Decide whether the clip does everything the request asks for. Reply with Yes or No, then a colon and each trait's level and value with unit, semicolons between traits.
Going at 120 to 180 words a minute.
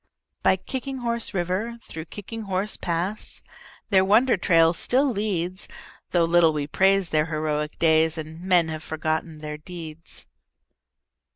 Yes: slow, 135 wpm